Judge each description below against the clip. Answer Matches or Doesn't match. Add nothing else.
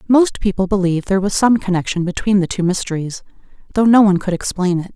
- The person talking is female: Matches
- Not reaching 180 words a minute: Doesn't match